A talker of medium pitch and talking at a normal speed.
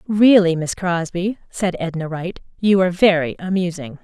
Yes: medium, 180 Hz; average, 150 wpm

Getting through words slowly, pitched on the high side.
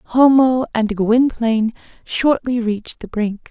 Yes: slow, 120 wpm; high, 235 Hz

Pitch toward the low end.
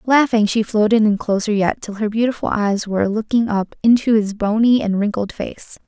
No: high, 215 Hz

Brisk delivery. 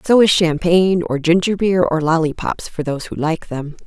No: average, 185 wpm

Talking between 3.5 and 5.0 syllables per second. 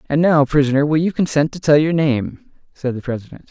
No: 5.6 syllables/s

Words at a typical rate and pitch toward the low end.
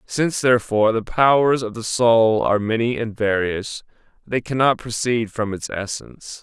Yes: average, 160 wpm; low, 115 Hz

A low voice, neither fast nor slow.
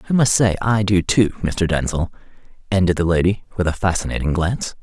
Yes: very low, 95 Hz; average, 185 wpm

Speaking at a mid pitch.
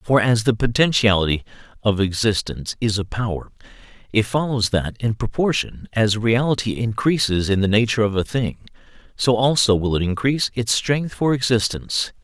No: low, 110 Hz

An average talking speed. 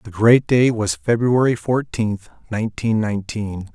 No: slow, 130 wpm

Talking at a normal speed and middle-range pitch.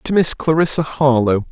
Yes: average, 160 wpm; medium, 145 Hz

